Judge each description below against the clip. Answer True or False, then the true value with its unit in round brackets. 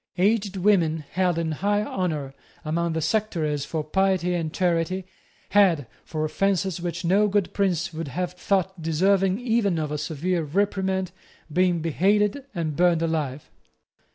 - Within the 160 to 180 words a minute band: False (145 wpm)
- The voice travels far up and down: False (3.3 semitones)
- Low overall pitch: False (180 Hz)